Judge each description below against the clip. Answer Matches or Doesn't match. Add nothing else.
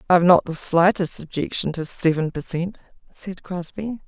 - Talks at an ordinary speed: Matches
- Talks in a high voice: Doesn't match